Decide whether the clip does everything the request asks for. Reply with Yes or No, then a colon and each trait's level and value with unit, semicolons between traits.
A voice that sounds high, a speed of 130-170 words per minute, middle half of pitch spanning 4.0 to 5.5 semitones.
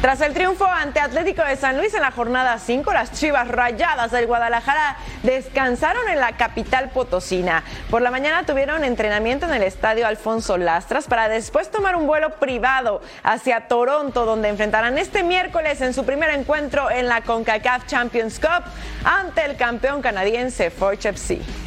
Yes: very high, 250 Hz; average, 165 wpm; average, 4.5 semitones